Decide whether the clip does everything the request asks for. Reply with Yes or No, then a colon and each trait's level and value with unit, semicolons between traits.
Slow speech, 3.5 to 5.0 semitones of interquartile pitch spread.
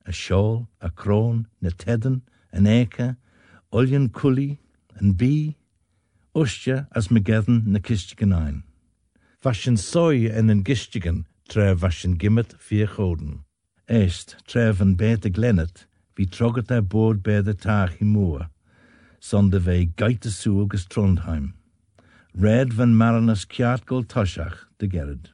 Yes: slow, 115 wpm; average, 4.0 semitones